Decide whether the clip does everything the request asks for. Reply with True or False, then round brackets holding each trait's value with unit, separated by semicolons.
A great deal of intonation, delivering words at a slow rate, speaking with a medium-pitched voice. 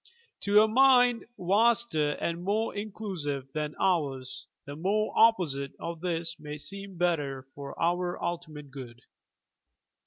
True (5.7 semitones; 125 wpm; 170 Hz)